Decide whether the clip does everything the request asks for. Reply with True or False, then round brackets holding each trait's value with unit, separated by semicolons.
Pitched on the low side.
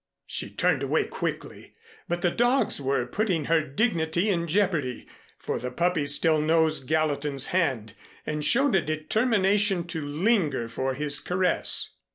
False (160 Hz)